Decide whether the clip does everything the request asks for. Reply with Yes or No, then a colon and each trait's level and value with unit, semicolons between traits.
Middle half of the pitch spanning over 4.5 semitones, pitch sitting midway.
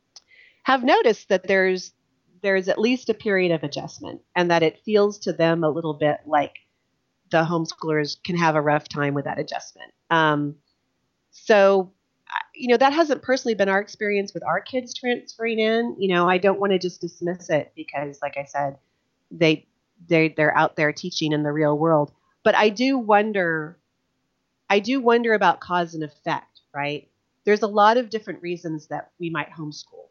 Yes: wide, 5.6 semitones; medium, 180 Hz